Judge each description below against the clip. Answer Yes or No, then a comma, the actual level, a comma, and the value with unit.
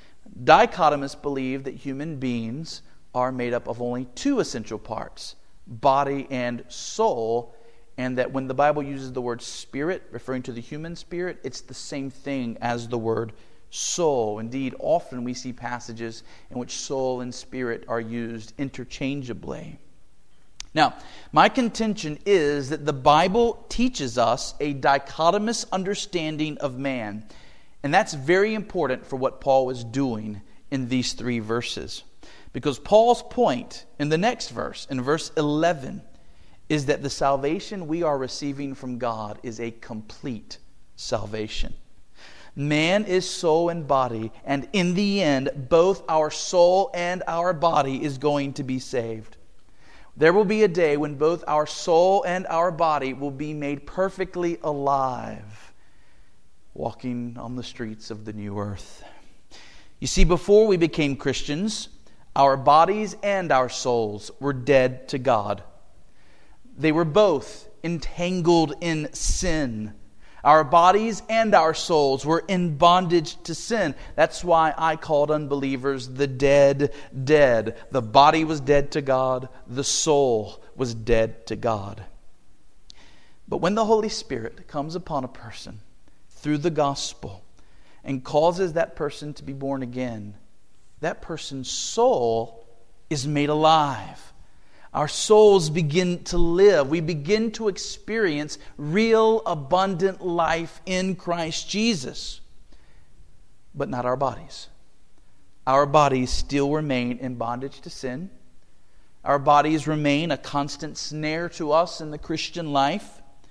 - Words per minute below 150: Yes, average, 140 wpm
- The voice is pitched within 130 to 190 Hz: Yes, medium, 140 Hz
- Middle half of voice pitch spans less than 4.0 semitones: No, average, 5.3 semitones